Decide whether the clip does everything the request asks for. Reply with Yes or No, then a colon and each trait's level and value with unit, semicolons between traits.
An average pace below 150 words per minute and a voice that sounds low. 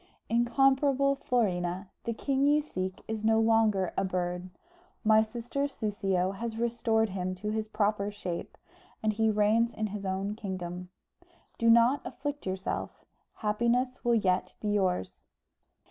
No: average, 140 wpm; high, 215 Hz